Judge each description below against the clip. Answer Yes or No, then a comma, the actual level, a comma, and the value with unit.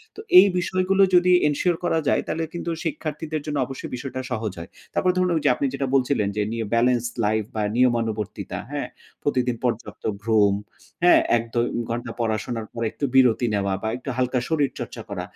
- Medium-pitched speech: No, low, 125 Hz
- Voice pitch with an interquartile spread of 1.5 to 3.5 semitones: No, wide, 5.4 semitones